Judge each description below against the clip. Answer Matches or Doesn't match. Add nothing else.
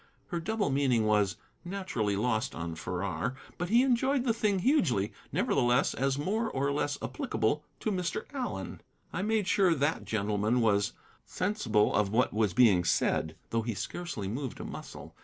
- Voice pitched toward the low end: Matches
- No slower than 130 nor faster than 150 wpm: Doesn't match